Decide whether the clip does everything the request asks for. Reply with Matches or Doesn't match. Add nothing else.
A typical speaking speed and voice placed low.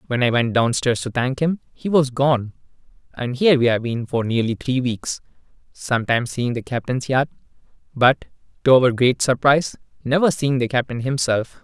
Matches